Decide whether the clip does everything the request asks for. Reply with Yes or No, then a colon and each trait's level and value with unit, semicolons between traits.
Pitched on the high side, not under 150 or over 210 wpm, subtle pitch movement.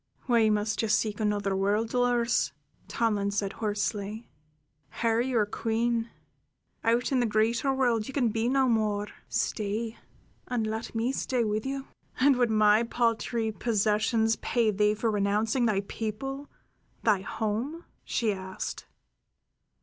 No: high, 225 Hz; average, 140 wpm; narrow, 2.2 semitones